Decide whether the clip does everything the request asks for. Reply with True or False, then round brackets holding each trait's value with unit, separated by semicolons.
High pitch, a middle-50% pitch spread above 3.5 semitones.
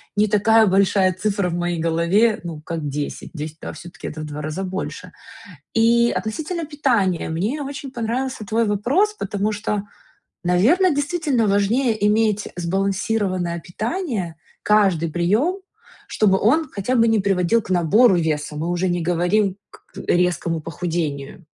True (195 Hz; 4.7 semitones)